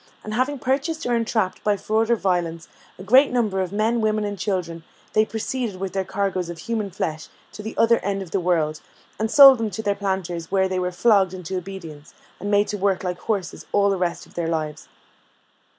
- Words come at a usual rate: No, fast, 215 wpm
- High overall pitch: Yes, high, 195 Hz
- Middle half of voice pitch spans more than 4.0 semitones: No, average, 3.4 semitones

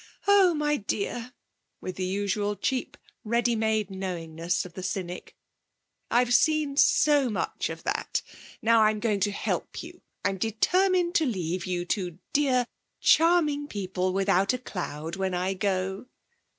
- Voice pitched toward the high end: Yes, high, 205 Hz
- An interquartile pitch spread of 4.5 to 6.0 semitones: Yes, wide, 5.5 semitones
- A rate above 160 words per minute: No, average, 145 wpm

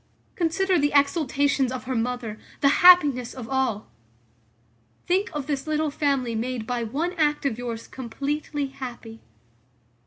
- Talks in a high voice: Yes, very high, 275 Hz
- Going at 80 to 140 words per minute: Yes, slow, 135 wpm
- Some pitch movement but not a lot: Yes, average, 3.4 semitones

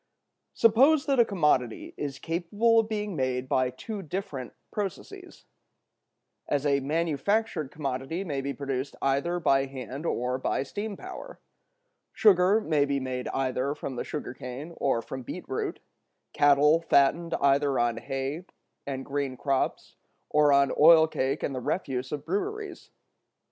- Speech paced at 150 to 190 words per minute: No, average, 140 wpm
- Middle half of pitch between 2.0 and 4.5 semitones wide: No, average, 5.1 semitones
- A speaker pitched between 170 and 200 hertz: No, medium, 145 Hz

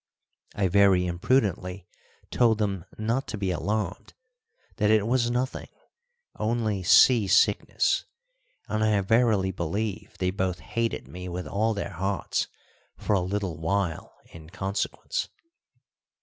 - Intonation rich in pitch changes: No, average, 3.1 semitones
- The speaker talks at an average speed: No, slow, 125 wpm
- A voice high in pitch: No, low, 100 Hz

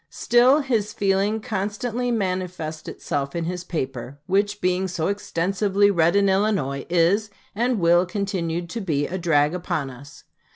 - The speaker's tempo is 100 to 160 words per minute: Yes, average, 150 wpm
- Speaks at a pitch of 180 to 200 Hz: Yes, medium, 185 Hz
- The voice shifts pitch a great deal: No, average, 3.7 semitones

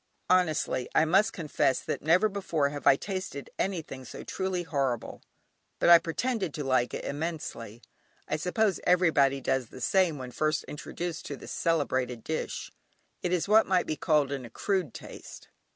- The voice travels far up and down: No, average, 4.9 semitones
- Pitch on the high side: No, medium, 155 Hz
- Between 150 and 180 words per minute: Yes, average, 165 wpm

